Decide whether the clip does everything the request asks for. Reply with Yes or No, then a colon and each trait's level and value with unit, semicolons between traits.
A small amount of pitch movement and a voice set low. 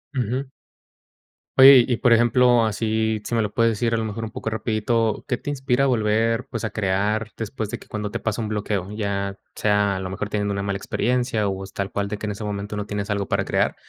Yes: narrow, 2.2 semitones; low, 110 Hz